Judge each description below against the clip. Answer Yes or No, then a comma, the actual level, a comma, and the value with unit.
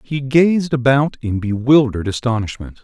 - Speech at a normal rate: No, slow, 125 wpm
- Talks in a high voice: No, low, 130 Hz